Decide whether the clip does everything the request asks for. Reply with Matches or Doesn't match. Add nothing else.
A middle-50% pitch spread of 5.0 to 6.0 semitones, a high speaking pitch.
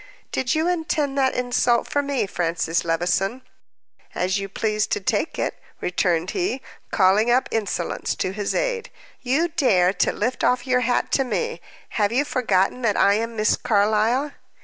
Matches